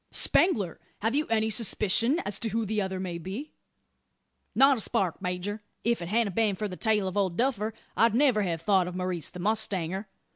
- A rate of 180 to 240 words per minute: Yes, average, 190 wpm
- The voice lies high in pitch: Yes, high, 205 Hz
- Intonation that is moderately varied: Yes, average, 3.6 semitones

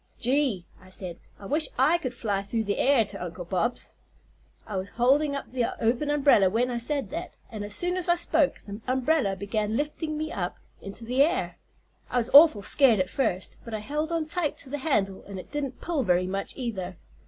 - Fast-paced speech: Yes, fast, 210 wpm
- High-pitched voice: Yes, high, 245 Hz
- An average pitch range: No, wide, 6.6 semitones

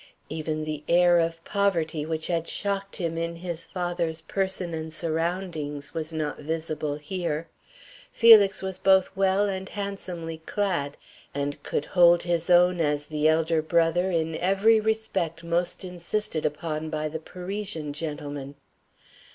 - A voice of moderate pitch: Yes, medium, 170 Hz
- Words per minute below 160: Yes, average, 140 wpm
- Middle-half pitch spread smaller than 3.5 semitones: Yes, average, 3.0 semitones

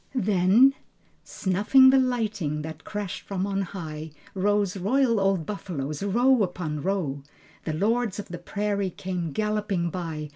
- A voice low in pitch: No, high, 195 Hz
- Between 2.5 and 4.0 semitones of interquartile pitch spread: Yes, average, 3.6 semitones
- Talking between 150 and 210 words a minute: No, average, 140 wpm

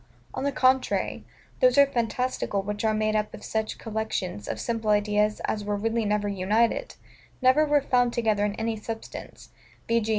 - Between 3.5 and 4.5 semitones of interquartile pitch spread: No, average, 2.8 semitones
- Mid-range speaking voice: No, high, 220 Hz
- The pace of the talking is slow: No, average, 175 wpm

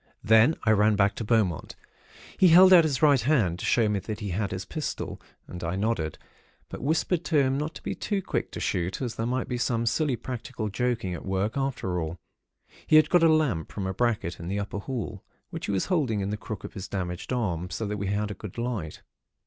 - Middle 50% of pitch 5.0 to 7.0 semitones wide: Yes, wide, 5.4 semitones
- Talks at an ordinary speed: No, fast, 235 wpm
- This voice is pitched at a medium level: No, low, 110 Hz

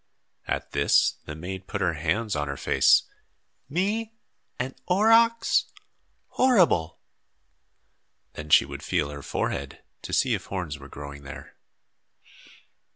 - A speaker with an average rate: No, slow, 130 wpm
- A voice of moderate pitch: No, very low, 90 Hz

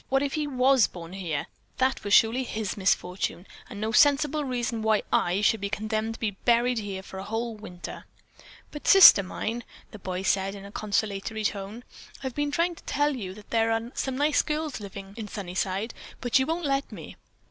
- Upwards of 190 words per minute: Yes, average, 200 wpm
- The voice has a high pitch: Yes, high, 220 Hz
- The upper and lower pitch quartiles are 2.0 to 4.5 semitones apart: No, average, 5.0 semitones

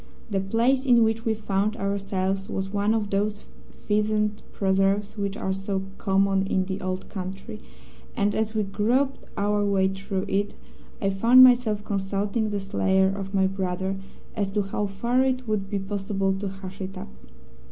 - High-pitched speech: Yes, high, 200 Hz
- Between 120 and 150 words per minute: No, average, 170 wpm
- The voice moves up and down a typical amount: No, narrow, 1.7 semitones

